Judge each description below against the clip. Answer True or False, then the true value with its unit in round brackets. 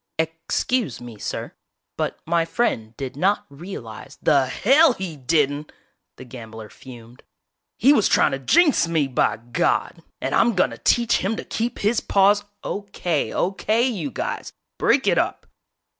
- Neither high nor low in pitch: True (165 Hz)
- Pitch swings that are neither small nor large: False (8.1 semitones)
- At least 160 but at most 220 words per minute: True (165 wpm)